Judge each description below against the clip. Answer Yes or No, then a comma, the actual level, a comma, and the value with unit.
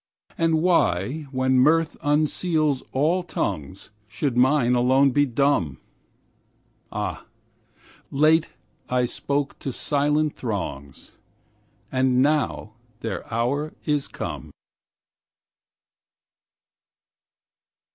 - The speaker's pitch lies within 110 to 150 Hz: Yes, medium, 140 Hz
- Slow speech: Yes, slow, 85 wpm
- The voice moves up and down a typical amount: Yes, average, 3.7 semitones